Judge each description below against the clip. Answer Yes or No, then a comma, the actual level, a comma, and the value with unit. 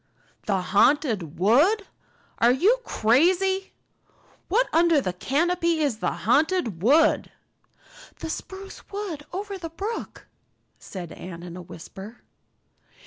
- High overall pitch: Yes, very high, 295 Hz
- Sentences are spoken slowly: Yes, slow, 115 wpm